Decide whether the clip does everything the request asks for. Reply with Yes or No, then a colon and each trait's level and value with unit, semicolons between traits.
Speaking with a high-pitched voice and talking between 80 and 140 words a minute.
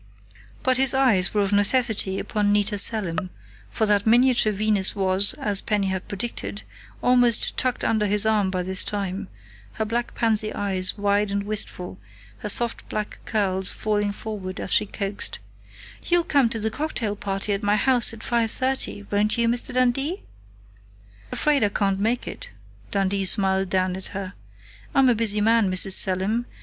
No: high, 210 Hz; average, 165 wpm